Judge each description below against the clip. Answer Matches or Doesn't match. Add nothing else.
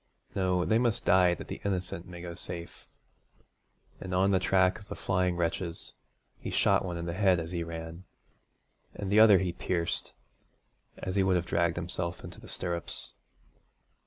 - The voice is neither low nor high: Doesn't match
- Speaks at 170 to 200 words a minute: Matches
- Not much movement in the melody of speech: Matches